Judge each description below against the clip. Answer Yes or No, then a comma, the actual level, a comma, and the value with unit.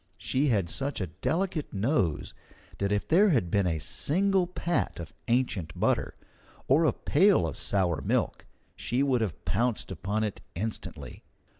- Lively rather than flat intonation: Yes, wide, 7.8 semitones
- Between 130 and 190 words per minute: Yes, average, 155 wpm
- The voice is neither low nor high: No, low, 115 Hz